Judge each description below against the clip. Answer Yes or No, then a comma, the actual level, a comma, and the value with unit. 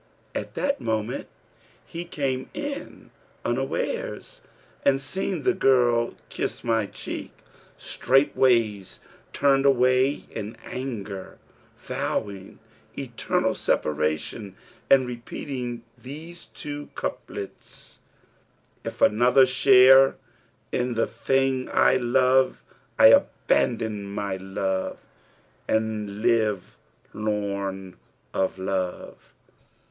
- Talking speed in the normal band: No, slow, 90 wpm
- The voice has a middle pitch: No, low, 120 Hz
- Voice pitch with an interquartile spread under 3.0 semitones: No, average, 4.7 semitones